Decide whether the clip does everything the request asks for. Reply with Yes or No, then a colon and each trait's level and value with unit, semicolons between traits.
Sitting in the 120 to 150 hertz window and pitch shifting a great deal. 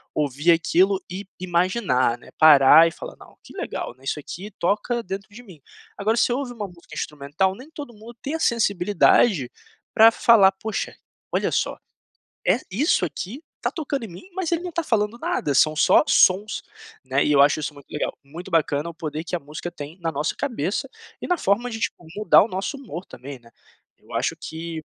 No: medium, 185 Hz; wide, 6.7 semitones